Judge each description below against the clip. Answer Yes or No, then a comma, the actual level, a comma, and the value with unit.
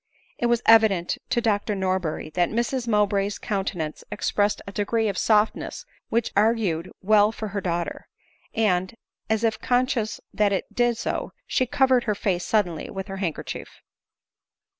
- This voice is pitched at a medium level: No, high, 210 Hz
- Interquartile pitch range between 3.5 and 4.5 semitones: No, average, 3.1 semitones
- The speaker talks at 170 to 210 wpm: No, average, 155 wpm